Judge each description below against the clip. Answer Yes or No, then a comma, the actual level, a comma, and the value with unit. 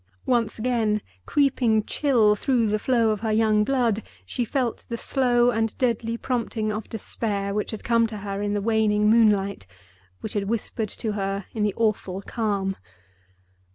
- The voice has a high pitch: Yes, high, 220 Hz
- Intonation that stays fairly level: Yes, narrow, 2.1 semitones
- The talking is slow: No, average, 165 wpm